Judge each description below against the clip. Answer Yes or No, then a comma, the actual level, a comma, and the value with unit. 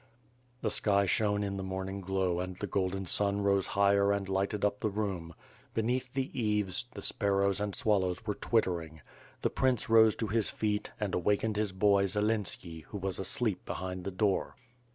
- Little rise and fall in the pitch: Yes, narrow, 2.1 semitones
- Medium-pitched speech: No, low, 100 Hz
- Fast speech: No, average, 180 wpm